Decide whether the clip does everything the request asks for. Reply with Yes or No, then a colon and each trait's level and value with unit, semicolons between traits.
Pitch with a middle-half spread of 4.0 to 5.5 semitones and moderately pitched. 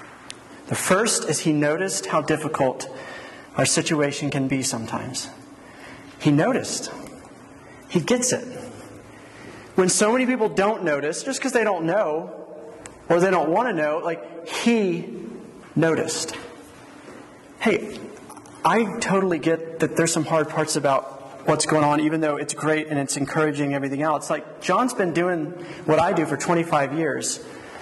No: average, 3.2 semitones; medium, 160 Hz